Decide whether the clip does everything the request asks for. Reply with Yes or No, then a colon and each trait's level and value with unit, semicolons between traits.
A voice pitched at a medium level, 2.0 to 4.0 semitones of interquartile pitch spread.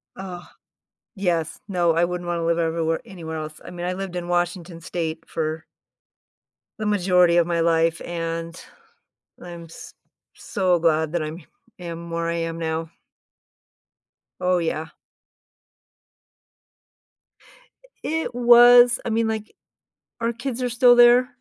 Yes: medium, 175 Hz; average, 3.3 semitones